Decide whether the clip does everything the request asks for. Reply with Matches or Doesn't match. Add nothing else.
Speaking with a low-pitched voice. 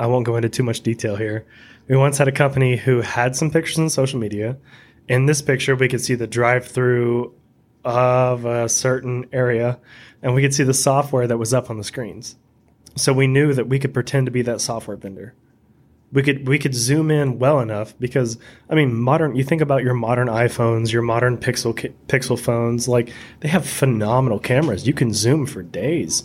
Matches